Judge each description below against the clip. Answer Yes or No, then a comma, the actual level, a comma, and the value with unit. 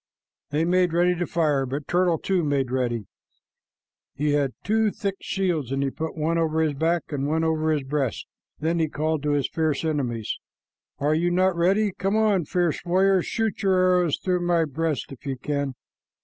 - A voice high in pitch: No, medium, 160 Hz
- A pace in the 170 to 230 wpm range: Yes, average, 190 wpm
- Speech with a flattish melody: No, average, 3.7 semitones